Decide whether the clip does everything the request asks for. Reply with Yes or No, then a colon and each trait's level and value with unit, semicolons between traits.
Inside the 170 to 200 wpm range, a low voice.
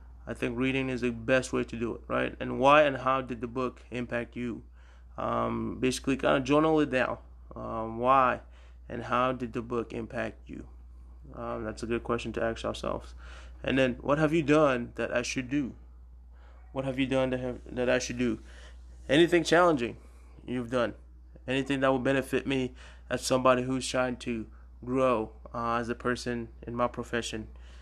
Yes: average, 185 wpm; low, 120 Hz